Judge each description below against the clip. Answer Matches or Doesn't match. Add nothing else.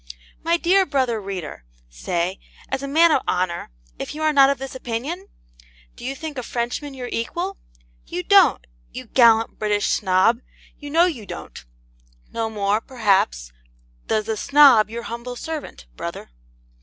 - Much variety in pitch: Matches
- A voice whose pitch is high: Matches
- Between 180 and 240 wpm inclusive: Doesn't match